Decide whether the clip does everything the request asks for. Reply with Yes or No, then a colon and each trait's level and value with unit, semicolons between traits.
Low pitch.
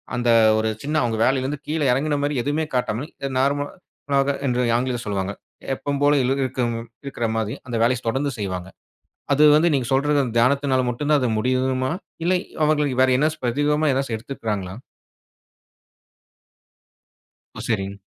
Yes: low, 130 Hz